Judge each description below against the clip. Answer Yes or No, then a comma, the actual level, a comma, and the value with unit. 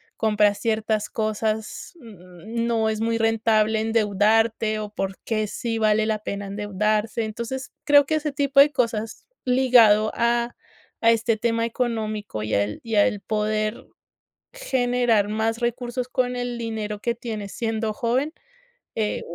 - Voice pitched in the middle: No, high, 225 Hz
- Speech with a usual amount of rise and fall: No, narrow, 1.9 semitones